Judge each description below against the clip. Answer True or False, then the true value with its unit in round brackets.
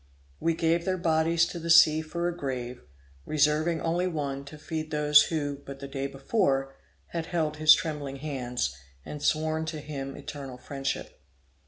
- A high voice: False (150 Hz)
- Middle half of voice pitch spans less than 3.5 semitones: True (2.8 semitones)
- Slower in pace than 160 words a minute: False (165 wpm)